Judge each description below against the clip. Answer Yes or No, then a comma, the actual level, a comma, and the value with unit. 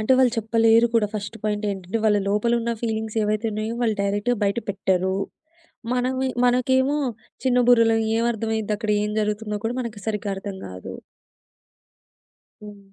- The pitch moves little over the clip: Yes, narrow, 2.2 semitones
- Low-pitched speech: No, high, 220 Hz